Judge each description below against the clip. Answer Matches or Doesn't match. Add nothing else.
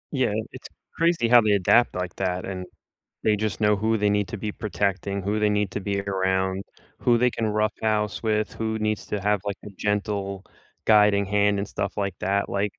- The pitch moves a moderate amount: Doesn't match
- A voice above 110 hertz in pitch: Doesn't match